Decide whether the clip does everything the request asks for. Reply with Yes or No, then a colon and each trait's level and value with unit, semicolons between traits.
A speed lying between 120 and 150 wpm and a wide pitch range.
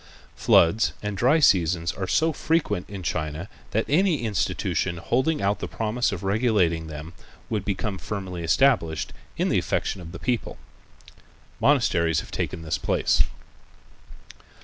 Yes: average, 145 wpm; wide, 6.0 semitones